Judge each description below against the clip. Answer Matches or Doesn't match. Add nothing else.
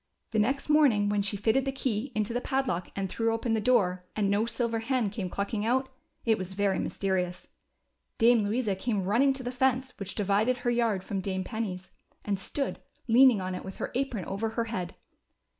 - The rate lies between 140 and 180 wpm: Doesn't match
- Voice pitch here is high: Matches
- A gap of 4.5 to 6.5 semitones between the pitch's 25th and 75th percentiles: Doesn't match